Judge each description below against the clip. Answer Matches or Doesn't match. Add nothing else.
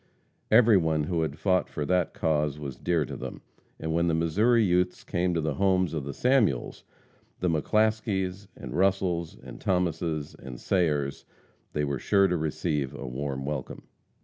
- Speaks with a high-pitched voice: Doesn't match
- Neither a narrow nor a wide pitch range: Matches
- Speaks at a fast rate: Doesn't match